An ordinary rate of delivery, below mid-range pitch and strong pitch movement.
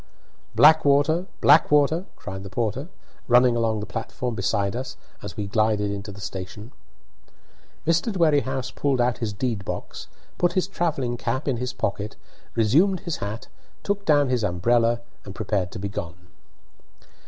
Yes: average, 150 wpm; low, 120 Hz; wide, 6.0 semitones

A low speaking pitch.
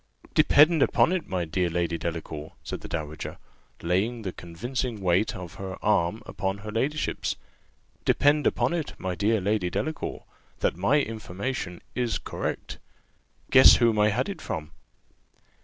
Yes: low, 105 Hz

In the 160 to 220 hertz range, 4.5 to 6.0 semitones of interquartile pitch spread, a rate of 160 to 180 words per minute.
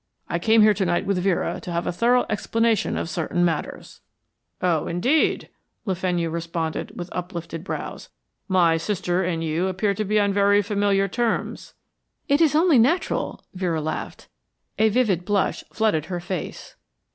No: high, 190 Hz; average, 3.8 semitones; average, 165 wpm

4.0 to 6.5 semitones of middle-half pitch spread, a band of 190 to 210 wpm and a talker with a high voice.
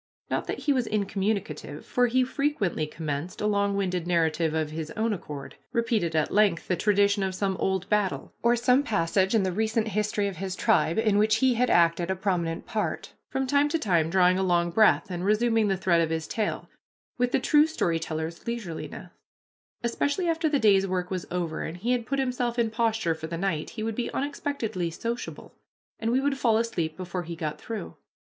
Yes: average, 5.3 semitones; average, 200 wpm; high, 200 Hz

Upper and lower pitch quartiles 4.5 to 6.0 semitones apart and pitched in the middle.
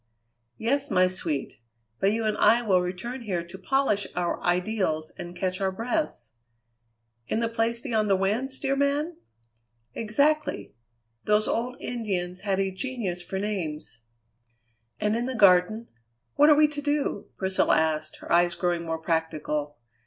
No: average, 5.2 semitones; high, 200 Hz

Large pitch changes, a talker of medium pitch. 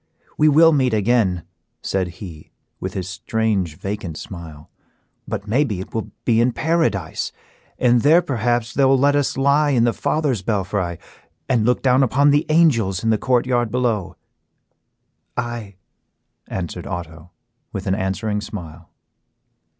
No: wide, 5.8 semitones; low, 110 Hz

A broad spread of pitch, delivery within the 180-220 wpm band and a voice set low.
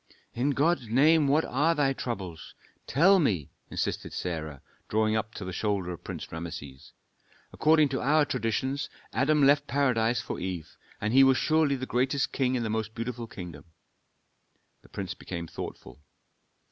No: wide, 6.4 semitones; average, 160 wpm; low, 120 Hz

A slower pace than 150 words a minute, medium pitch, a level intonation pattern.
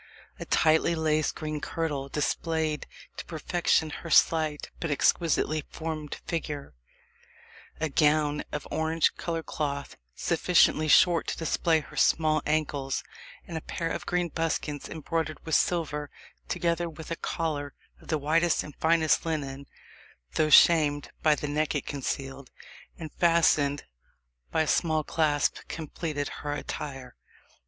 Yes: slow, 135 wpm; medium, 155 Hz; narrow, 1.8 semitones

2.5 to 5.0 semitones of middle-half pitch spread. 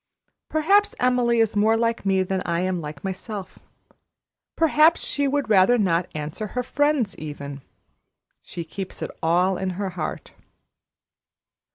No: wide, 5.6 semitones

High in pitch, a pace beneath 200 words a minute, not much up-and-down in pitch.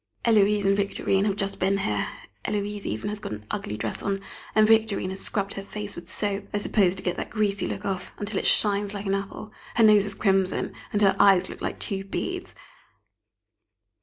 No: high, 200 Hz; fast, 205 wpm; narrow, 1.2 semitones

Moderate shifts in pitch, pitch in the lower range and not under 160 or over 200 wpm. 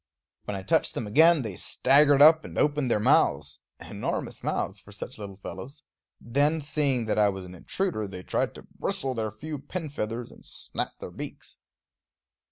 No: wide, 6.4 semitones; low, 120 Hz; average, 175 wpm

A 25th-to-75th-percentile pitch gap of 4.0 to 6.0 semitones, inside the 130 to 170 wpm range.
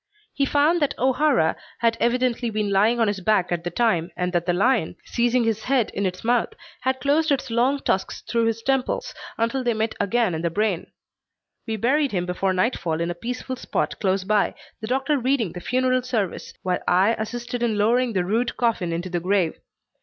No: average, 5.1 semitones; average, 200 wpm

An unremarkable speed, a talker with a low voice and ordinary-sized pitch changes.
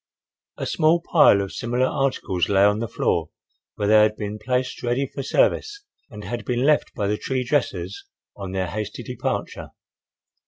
Yes: average, 170 wpm; low, 115 Hz; average, 4.2 semitones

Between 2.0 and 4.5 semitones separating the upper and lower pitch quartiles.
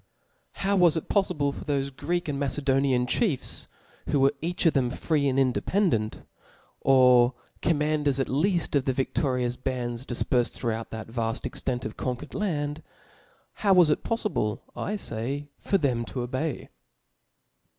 Yes: average, 4.2 semitones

